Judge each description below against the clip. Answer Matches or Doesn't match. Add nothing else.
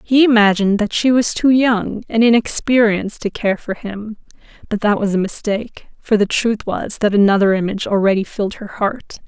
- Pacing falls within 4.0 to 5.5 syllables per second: Matches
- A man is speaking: Doesn't match